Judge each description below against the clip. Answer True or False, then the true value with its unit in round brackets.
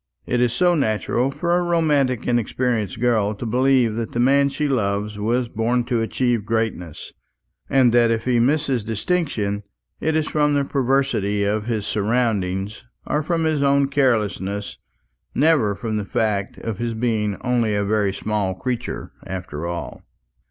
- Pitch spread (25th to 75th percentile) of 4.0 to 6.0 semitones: True (4.5 semitones)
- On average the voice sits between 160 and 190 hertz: False (115 Hz)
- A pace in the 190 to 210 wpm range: False (160 wpm)